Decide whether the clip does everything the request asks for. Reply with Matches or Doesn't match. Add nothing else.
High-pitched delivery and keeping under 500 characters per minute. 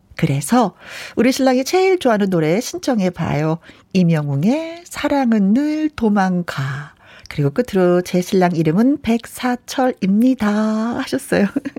Matches